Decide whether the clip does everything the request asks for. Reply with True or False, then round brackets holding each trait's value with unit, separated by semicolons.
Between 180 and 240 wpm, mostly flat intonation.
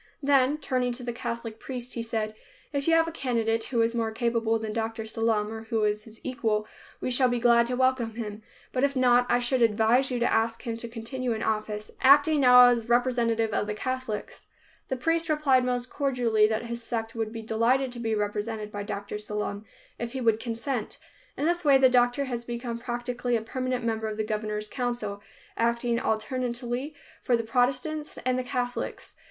True (200 wpm; 2.3 semitones)